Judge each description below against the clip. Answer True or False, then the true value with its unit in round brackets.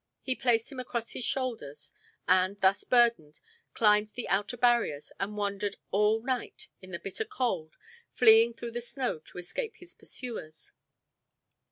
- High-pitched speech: True (225 Hz)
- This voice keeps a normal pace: True (150 wpm)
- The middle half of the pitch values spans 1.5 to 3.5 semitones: False (4.2 semitones)